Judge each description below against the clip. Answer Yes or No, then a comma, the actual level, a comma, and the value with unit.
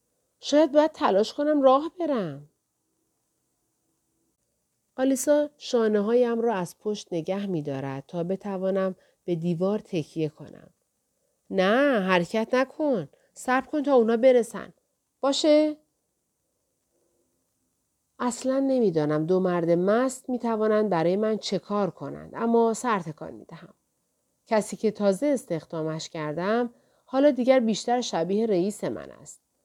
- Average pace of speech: Yes, average, 115 wpm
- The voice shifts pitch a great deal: Yes, wide, 6.4 semitones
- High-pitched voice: Yes, high, 215 Hz